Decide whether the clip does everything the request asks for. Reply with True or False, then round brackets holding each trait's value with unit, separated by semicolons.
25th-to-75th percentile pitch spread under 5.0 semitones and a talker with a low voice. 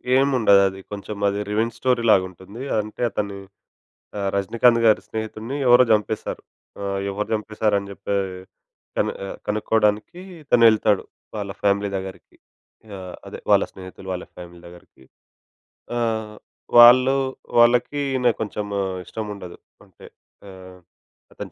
True (3.0 semitones; 105 Hz)